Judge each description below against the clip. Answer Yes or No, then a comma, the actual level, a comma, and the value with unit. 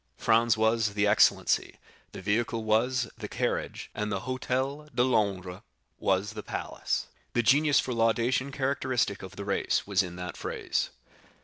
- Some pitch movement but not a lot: Yes, average, 4.0 semitones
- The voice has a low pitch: Yes, low, 110 Hz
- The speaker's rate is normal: Yes, average, 150 wpm